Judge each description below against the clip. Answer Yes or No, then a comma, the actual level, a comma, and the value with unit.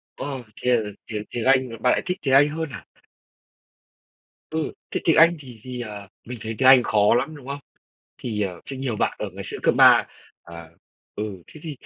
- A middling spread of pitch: Yes, average, 4.7 semitones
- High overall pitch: No, low, 125 Hz